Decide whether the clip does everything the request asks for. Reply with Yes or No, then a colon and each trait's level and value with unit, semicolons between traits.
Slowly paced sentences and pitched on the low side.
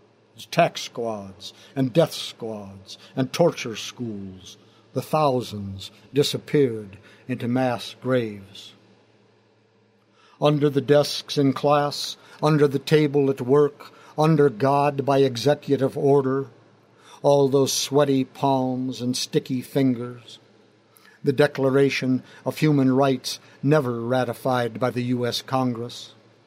Yes: slow, 105 wpm; low, 130 Hz